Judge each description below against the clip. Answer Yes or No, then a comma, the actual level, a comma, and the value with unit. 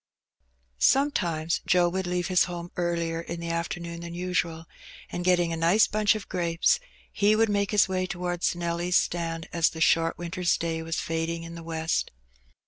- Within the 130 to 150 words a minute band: No, average, 180 wpm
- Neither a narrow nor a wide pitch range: No, narrow, 1.4 semitones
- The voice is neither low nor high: Yes, medium, 170 Hz